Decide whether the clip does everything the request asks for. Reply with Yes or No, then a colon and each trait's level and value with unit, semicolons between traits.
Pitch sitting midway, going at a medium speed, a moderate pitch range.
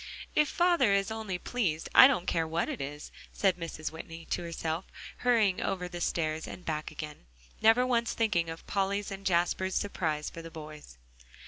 Yes: medium, 180 Hz; average, 180 wpm; average, 4.2 semitones